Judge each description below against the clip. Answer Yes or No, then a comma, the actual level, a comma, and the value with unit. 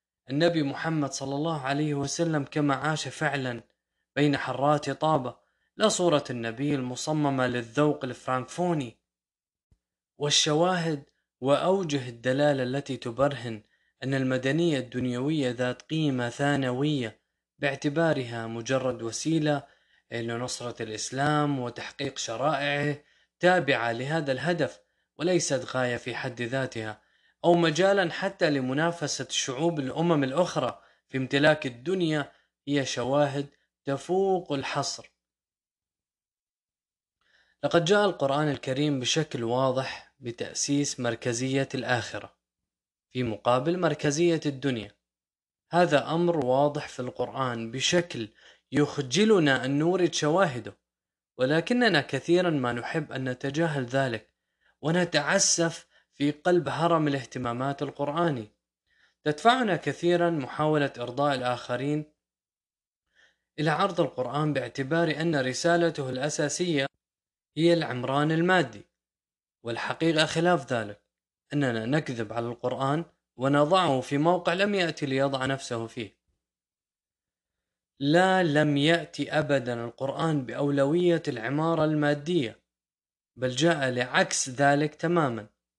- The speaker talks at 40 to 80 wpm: No, average, 95 wpm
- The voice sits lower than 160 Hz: Yes, medium, 140 Hz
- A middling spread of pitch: Yes, average, 4.1 semitones